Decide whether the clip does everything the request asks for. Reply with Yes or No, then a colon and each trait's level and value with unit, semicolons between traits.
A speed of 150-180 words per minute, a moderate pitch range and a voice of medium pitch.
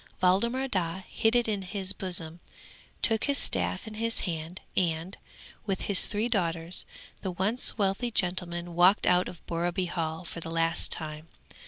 Yes: average, 160 wpm; average, 3.5 semitones; medium, 180 Hz